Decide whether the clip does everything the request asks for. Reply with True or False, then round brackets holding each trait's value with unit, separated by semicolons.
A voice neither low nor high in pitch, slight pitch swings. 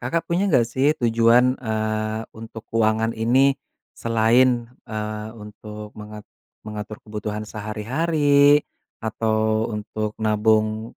False (110 Hz; 2.0 semitones)